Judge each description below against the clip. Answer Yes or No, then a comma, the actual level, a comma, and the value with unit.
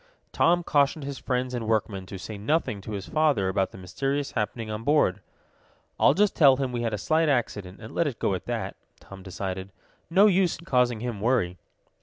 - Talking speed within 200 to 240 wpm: Yes, fast, 205 wpm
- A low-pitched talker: Yes, low, 120 Hz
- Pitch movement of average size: No, wide, 6.4 semitones